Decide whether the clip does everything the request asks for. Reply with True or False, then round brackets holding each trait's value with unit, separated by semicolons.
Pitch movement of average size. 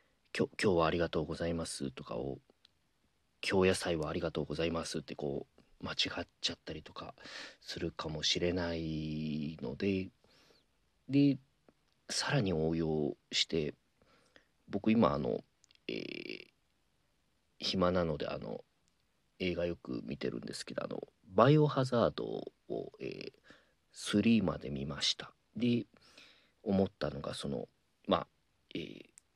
True (4.1 semitones)